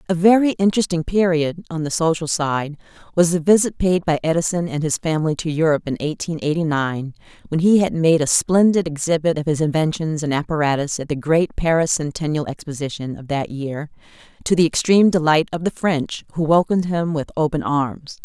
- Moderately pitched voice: Yes, medium, 160 Hz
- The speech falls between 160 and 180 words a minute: No, average, 190 wpm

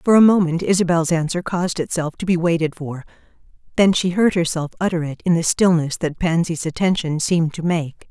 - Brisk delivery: No, average, 195 wpm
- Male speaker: No, female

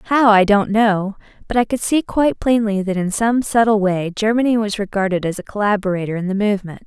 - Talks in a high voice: Yes, high, 210 Hz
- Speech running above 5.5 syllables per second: Yes, 5.7 syllables/s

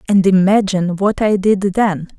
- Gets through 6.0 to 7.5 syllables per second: No, 4.5 syllables/s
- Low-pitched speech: No, high, 195 Hz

